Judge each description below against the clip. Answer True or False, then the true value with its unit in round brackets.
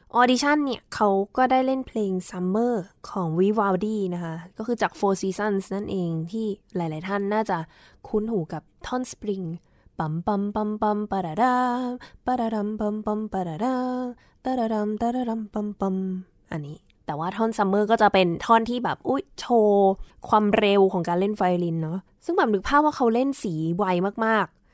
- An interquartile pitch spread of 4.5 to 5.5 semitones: False (3.6 semitones)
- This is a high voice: True (210 Hz)